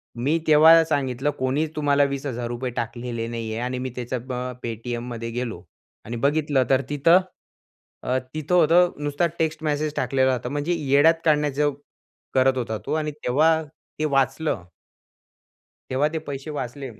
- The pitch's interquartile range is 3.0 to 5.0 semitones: Yes, average, 3.6 semitones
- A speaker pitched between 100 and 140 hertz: Yes, low, 135 Hz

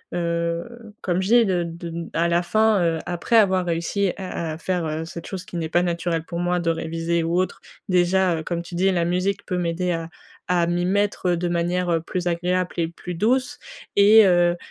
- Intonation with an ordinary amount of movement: No, narrow, 1.8 semitones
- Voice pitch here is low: No, medium, 175 Hz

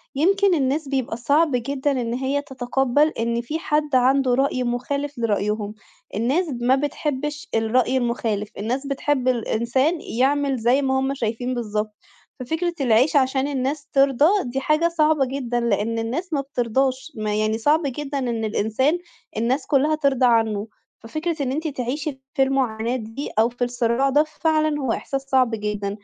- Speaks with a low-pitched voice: No, very high, 265 Hz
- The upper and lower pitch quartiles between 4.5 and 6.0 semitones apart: No, average, 3.5 semitones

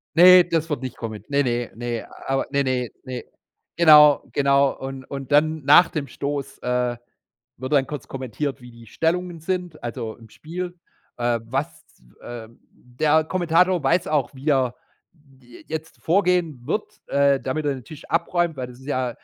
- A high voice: No, medium, 140 Hz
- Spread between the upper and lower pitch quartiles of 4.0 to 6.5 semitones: Yes, average, 4.3 semitones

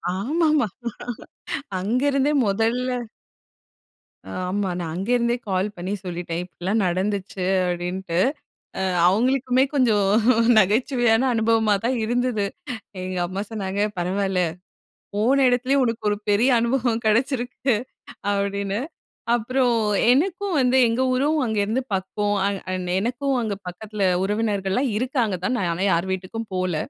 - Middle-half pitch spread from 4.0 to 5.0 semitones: Yes, average, 4.6 semitones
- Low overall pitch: No, high, 220 Hz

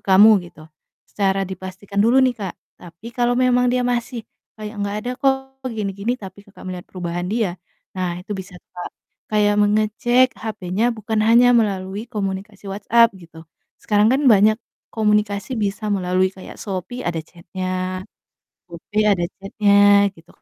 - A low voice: No, high, 205 Hz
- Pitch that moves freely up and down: No, average, 3.3 semitones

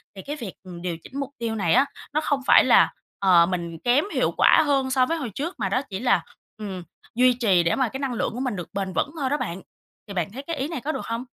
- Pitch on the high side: Yes, high, 240 Hz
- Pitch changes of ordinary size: No, wide, 6.3 semitones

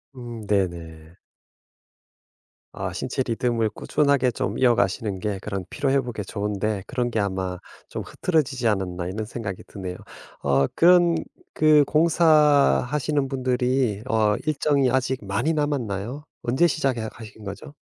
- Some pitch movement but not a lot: No, wide, 5.9 semitones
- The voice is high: No, low, 120 Hz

